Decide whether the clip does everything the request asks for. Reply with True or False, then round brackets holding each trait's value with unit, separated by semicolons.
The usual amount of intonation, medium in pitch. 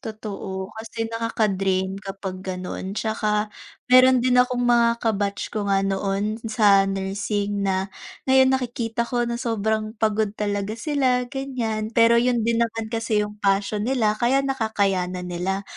False (3.0 semitones; 215 Hz)